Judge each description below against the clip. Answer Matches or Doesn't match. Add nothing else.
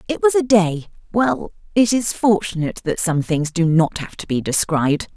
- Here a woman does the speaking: Matches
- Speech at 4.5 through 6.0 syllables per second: Matches